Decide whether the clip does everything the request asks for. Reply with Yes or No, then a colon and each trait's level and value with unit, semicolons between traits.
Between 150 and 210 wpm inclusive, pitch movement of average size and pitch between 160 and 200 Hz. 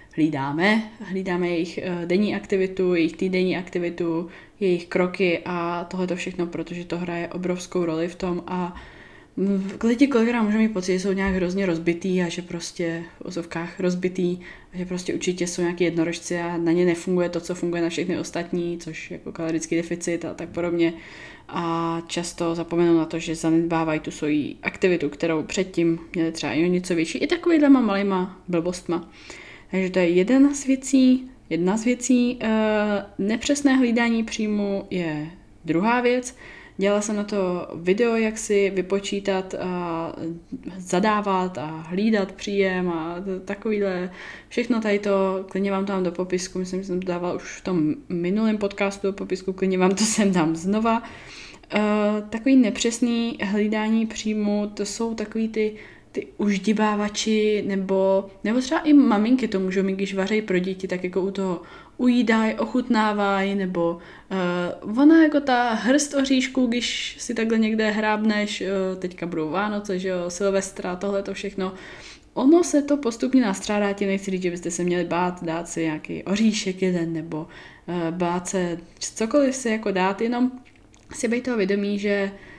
Yes: average, 165 wpm; average, 3.6 semitones; high, 190 Hz